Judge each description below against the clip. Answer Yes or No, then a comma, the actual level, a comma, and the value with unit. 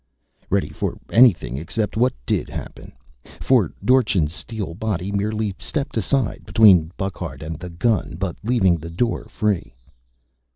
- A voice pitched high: No, low, 100 Hz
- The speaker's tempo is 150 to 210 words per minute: No, slow, 135 wpm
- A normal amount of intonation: Yes, average, 4.9 semitones